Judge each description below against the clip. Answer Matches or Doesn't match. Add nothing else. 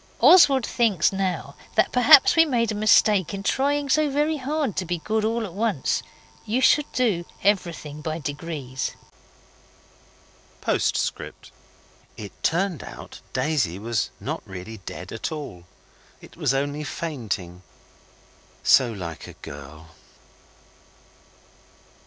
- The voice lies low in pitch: Doesn't match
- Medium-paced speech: Doesn't match